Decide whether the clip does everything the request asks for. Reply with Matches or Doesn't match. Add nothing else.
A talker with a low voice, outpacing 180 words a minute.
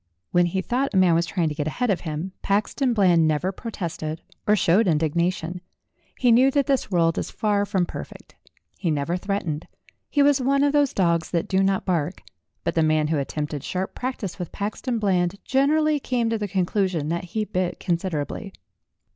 Doesn't match